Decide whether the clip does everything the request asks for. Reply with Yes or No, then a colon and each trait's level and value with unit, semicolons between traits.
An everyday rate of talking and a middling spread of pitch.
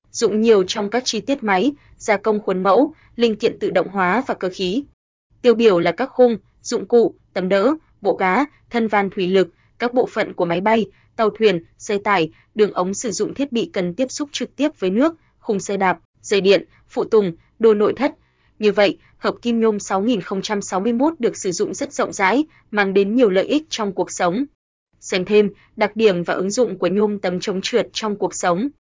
Yes: average, 210 wpm; average, 4.3 semitones